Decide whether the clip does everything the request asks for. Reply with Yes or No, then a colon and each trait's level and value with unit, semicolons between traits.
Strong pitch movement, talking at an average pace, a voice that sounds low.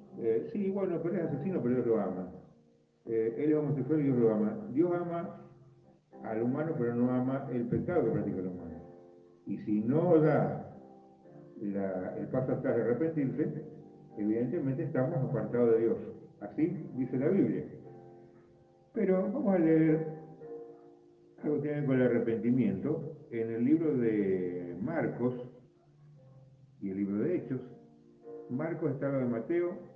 Yes: wide, 6.5 semitones; average, 155 wpm; low, 130 Hz